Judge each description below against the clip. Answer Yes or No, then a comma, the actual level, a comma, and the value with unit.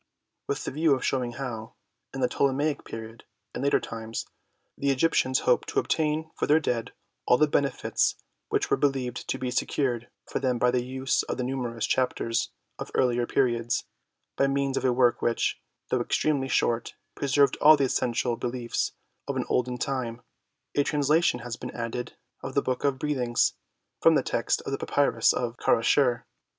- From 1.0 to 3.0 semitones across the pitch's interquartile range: Yes, narrow, 2.6 semitones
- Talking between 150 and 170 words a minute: No, average, 185 wpm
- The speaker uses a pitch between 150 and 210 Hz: No, low, 130 Hz